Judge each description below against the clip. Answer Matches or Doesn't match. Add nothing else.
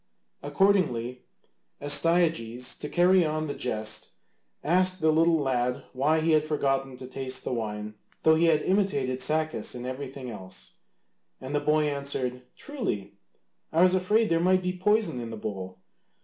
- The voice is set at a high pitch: Doesn't match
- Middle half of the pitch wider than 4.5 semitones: Matches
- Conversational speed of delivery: Matches